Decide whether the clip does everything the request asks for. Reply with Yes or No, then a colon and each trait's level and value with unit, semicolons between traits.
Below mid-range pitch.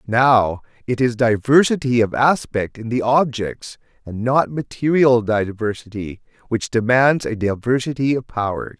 Yes: low, 120 Hz